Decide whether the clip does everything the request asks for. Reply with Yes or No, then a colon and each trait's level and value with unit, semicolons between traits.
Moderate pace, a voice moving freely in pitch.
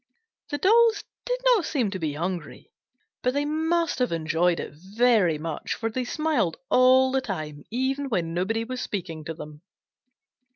Yes: average, 165 wpm; wide, 8.9 semitones